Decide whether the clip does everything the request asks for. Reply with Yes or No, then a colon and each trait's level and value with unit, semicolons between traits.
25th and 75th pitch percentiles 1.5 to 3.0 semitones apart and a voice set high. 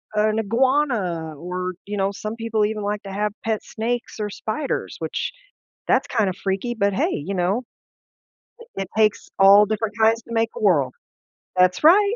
Yes: average, 2.7 semitones; high, 210 Hz